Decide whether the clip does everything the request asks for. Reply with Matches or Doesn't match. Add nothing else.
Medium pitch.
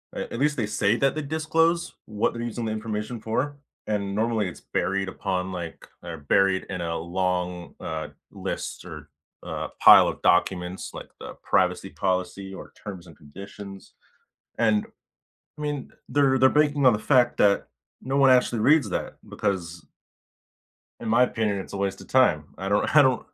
Doesn't match